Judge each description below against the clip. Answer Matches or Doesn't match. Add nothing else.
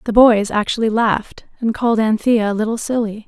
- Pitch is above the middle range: Matches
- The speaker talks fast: Doesn't match